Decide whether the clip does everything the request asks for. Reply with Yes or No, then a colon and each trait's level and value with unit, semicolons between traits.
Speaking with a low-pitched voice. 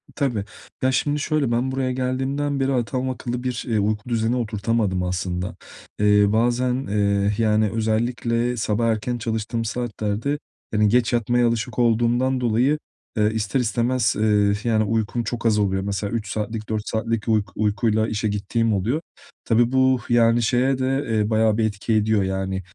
Yes: low, 115 Hz